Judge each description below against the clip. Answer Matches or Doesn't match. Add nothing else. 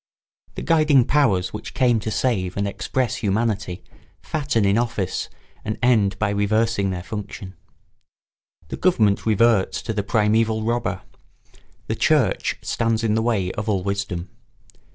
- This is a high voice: Doesn't match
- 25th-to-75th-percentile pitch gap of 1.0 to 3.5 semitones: Matches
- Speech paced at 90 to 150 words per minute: Matches